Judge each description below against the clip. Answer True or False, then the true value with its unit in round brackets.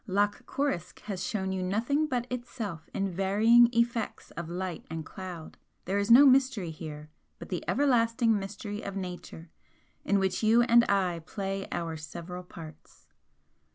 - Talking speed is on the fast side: False (155 wpm)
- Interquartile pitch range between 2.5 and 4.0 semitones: False (4.7 semitones)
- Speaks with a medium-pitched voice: False (195 Hz)